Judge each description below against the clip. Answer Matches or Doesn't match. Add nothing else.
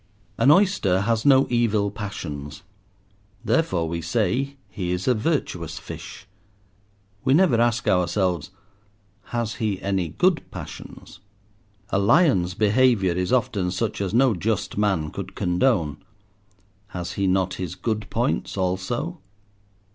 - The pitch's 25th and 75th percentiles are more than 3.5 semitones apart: Matches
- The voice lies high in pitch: Doesn't match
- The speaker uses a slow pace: Matches